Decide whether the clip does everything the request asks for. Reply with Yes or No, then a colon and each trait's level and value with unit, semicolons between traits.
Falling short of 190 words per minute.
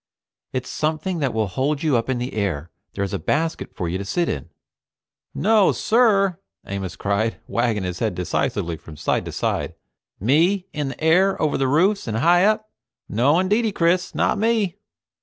Yes: average, 180 wpm